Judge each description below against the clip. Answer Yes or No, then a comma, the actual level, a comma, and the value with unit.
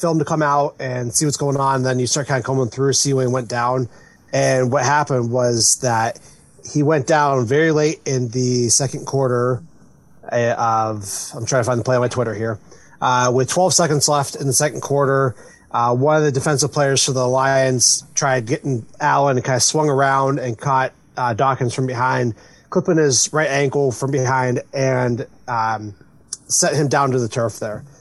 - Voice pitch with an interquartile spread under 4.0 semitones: Yes, narrow, 2.5 semitones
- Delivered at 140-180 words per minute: No, average, 200 wpm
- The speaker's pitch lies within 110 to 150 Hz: Yes, low, 135 Hz